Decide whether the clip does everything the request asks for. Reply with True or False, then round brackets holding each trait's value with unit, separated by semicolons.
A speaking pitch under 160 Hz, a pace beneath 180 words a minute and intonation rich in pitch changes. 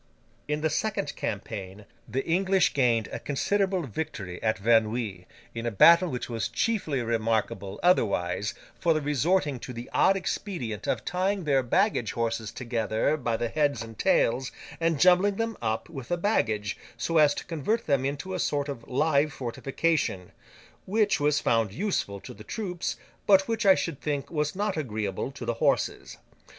True (140 Hz; 165 wpm; 7.6 semitones)